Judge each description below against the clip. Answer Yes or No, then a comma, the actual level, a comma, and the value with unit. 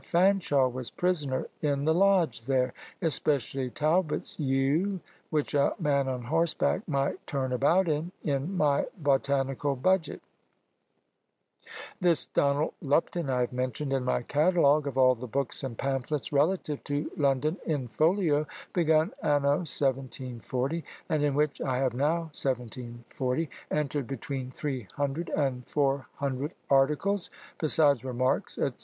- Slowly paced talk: Yes, slow, 130 wpm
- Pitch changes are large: No, average, 3.0 semitones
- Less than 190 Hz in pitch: Yes, medium, 140 Hz